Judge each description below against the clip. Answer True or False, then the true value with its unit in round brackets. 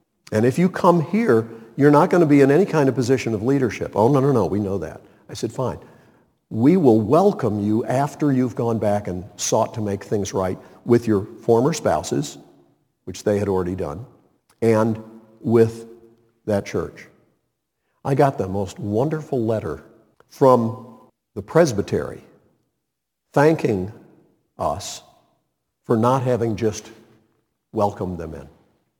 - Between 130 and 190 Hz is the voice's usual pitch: False (115 Hz)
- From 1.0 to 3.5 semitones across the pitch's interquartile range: False (4.6 semitones)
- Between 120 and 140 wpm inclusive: False (150 wpm)